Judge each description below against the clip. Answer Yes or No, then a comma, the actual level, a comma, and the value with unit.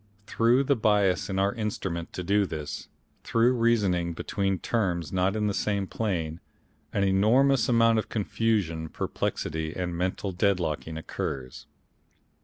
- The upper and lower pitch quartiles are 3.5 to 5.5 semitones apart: Yes, average, 4.4 semitones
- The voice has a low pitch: Yes, very low, 95 Hz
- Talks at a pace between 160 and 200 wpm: No, slow, 135 wpm